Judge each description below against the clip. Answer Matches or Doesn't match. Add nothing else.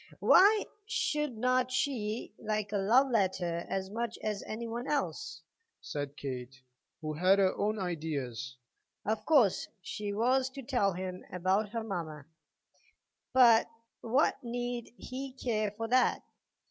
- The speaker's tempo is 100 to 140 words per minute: Matches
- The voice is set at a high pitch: Matches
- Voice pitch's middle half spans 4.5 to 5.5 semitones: Matches